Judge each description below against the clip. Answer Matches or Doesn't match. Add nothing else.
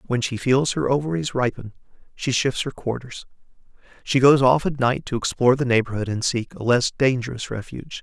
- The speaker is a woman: Doesn't match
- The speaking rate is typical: Matches